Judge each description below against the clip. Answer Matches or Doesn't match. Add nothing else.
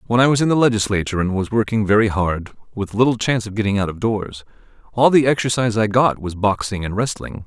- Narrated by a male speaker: Matches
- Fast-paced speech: Matches